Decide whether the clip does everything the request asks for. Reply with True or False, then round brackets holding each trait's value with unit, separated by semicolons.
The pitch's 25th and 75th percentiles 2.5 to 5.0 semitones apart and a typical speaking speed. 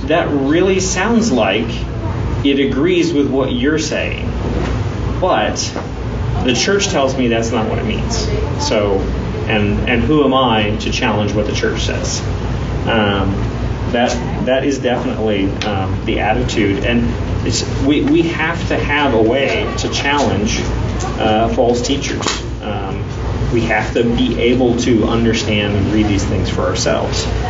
True (2.9 semitones; 150 wpm)